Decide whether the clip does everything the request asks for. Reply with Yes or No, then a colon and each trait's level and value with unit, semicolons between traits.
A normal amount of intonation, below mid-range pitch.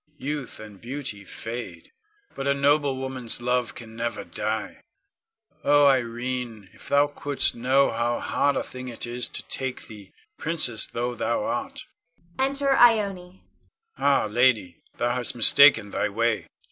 Yes: average, 3.7 semitones; low, 125 Hz